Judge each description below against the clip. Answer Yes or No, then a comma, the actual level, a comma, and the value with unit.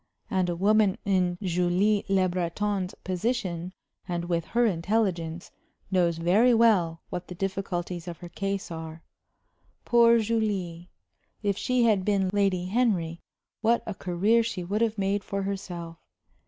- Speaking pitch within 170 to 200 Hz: Yes, high, 190 Hz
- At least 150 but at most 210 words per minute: No, average, 140 wpm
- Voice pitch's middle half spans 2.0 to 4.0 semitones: Yes, average, 3.2 semitones